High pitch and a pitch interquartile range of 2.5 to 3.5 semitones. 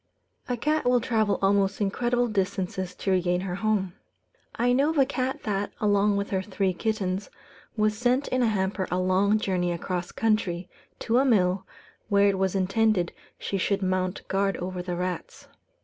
Yes: high, 200 Hz; average, 3.0 semitones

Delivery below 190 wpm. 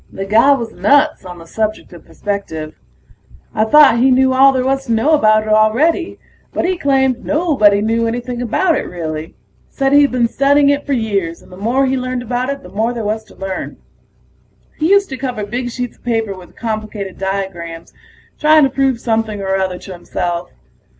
No: average, 195 wpm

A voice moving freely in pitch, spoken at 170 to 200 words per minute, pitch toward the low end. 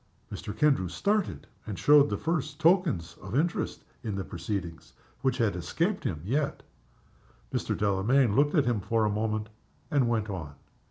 No: wide, 6.9 semitones; average, 160 wpm; low, 115 Hz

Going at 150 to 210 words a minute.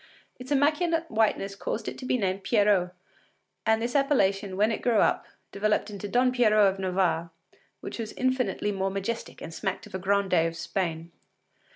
Yes: average, 175 wpm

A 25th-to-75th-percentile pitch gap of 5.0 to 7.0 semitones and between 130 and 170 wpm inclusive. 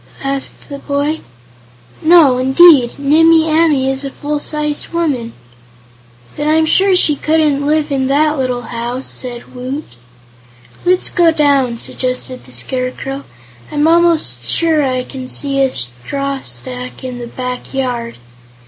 No: average, 3.4 semitones; average, 140 wpm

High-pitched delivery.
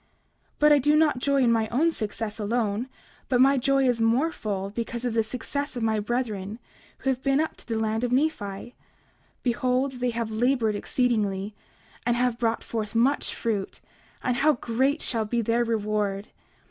Yes: high, 235 Hz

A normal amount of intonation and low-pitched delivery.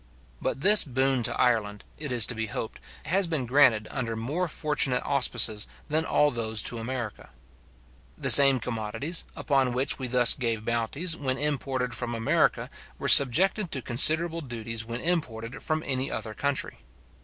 Yes: average, 4.2 semitones; low, 130 Hz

